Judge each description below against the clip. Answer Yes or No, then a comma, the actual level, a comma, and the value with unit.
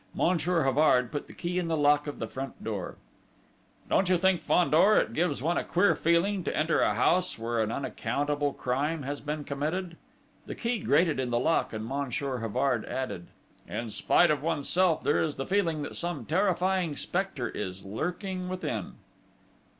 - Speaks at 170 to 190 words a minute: Yes, average, 175 wpm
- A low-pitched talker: No, medium, 150 Hz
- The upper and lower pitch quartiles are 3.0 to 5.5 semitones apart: Yes, average, 5.1 semitones